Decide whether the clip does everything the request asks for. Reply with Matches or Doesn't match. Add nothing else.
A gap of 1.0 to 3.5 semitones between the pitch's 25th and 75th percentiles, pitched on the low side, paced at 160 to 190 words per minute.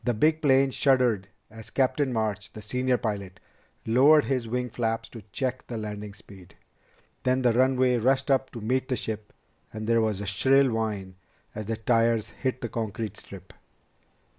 Matches